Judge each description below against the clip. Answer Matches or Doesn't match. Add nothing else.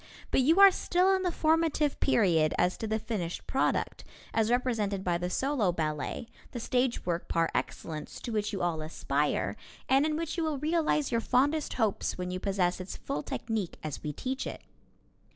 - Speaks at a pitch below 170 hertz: Doesn't match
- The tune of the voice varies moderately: Doesn't match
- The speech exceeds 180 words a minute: Matches